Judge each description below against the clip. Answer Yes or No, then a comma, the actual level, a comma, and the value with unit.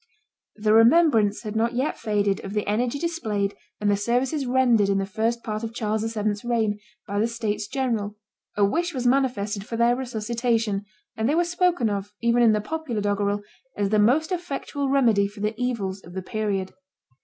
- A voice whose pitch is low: No, high, 220 Hz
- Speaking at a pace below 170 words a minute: No, average, 190 wpm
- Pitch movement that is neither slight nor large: Yes, average, 3.3 semitones